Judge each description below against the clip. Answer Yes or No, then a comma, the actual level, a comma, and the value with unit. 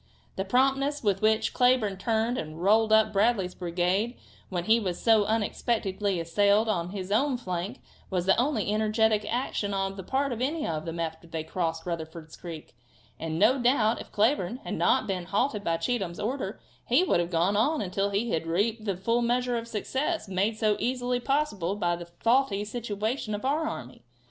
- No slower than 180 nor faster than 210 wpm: Yes, average, 190 wpm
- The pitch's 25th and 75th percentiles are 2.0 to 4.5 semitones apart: No, average, 4.9 semitones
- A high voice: Yes, high, 210 Hz